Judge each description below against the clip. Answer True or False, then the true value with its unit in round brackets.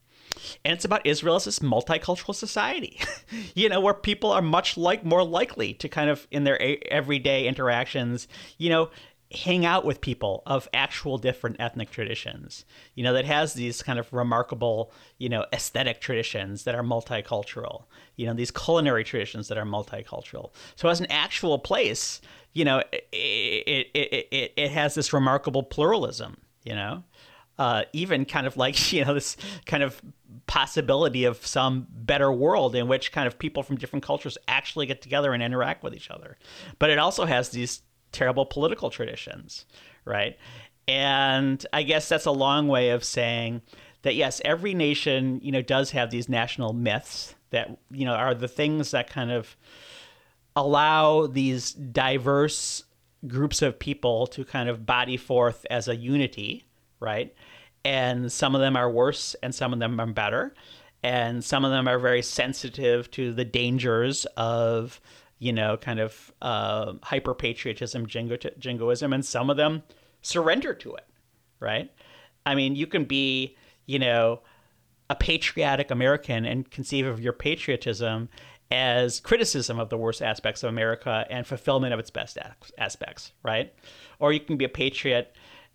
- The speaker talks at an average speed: True (165 wpm)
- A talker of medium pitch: False (130 Hz)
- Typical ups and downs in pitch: True (3.4 semitones)